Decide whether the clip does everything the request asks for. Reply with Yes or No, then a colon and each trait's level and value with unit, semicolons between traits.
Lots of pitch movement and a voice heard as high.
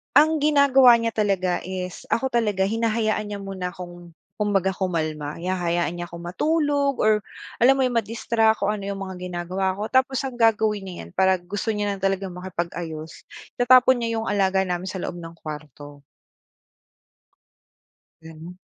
No: average, 4.5 semitones; high, 195 Hz